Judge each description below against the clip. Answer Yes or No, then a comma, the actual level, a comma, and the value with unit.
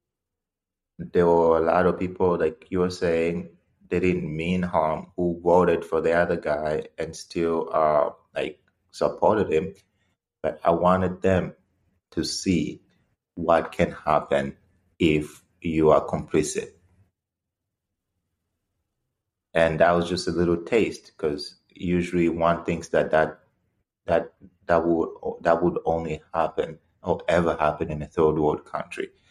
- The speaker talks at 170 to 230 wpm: No, average, 140 wpm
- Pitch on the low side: Yes, very low, 85 Hz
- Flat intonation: Yes, narrow, 1.8 semitones